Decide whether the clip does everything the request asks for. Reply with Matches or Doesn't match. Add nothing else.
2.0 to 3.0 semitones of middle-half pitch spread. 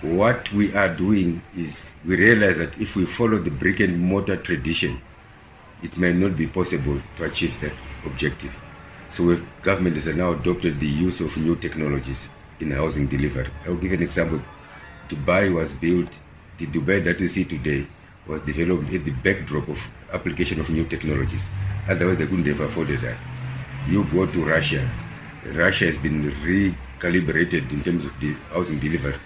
Doesn't match